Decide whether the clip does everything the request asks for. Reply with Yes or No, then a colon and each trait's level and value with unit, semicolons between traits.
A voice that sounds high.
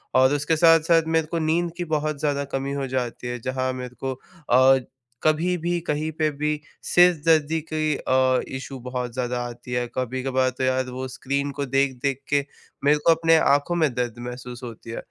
No: low, 135 Hz